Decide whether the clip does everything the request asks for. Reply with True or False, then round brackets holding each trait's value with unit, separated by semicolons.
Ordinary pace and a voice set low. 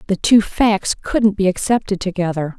False (160 wpm; 195 Hz)